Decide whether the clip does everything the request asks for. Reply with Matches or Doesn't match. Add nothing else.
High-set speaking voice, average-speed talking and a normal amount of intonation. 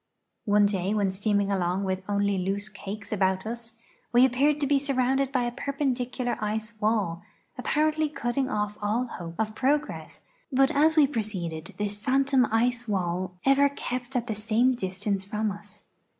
Matches